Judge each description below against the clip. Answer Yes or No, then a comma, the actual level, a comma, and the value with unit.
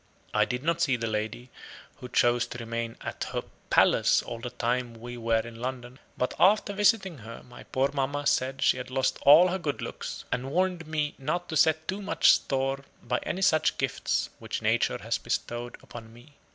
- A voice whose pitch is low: Yes, low, 130 Hz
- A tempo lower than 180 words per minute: No, average, 195 wpm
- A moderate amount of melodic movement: Yes, average, 4.8 semitones